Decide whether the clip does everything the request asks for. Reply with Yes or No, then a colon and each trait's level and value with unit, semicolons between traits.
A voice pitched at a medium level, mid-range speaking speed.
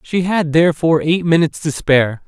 Yes: medium, 160 Hz; average, 185 wpm